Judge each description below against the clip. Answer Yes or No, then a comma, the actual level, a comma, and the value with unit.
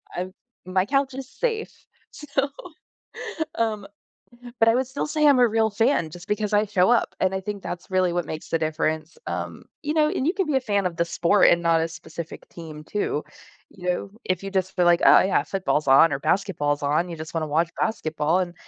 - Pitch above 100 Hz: Yes, medium, 185 Hz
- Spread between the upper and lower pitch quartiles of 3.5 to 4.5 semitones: No, wide, 5.4 semitones